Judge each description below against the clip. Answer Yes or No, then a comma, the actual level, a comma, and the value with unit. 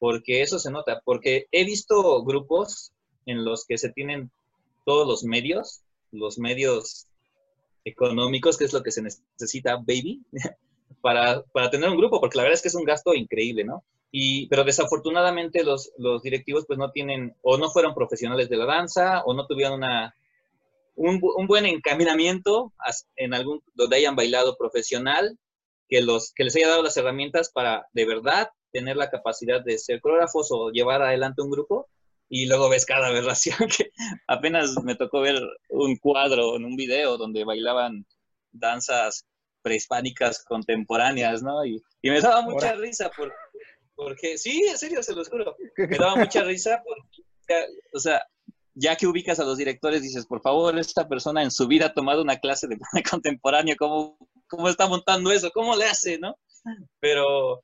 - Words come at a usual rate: Yes, average, 170 wpm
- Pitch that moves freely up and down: Yes, wide, 8.4 semitones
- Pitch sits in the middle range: Yes, medium, 155 Hz